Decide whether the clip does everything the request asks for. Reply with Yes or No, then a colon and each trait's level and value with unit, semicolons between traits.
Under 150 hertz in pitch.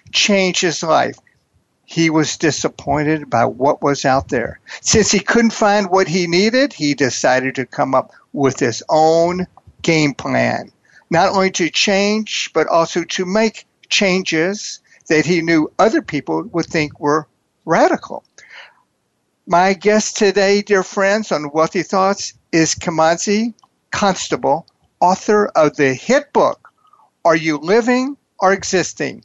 No: medium, 175 Hz